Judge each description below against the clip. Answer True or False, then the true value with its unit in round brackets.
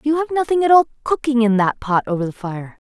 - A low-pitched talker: False (255 Hz)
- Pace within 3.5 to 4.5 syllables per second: False (6.0 syllables/s)